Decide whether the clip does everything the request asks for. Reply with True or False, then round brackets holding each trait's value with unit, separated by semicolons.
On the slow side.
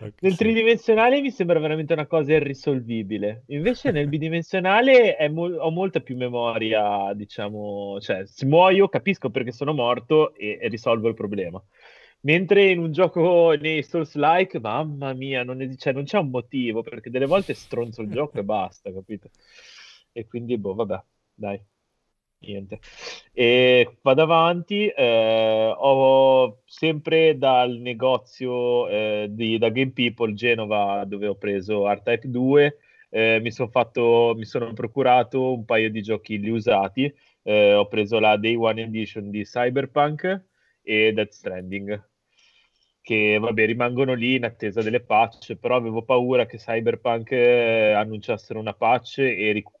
False (145 wpm)